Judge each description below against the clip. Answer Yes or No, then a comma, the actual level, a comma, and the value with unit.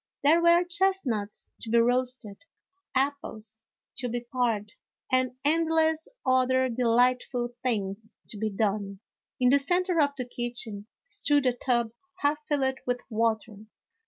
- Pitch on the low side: No, very high, 250 Hz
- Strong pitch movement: No, average, 4.1 semitones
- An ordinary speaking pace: No, slow, 130 wpm